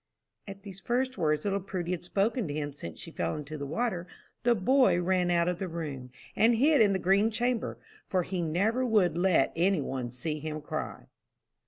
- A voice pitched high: No, medium, 180 Hz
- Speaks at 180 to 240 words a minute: Yes, average, 200 wpm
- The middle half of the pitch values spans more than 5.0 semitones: Yes, wide, 5.5 semitones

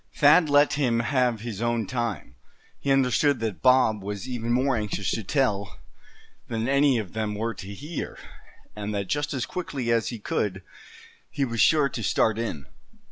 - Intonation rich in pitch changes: No, average, 4.4 semitones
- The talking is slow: No, average, 175 wpm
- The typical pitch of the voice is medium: No, low, 115 Hz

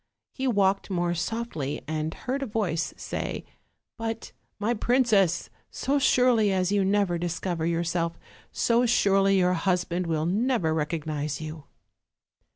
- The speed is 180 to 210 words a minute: No, slow, 135 wpm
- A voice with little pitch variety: No, average, 5.3 semitones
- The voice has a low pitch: No, medium, 185 Hz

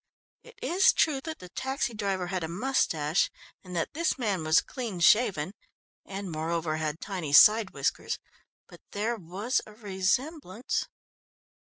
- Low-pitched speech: No, high, 195 Hz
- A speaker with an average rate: Yes, average, 145 wpm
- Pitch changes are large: Yes, wide, 6.0 semitones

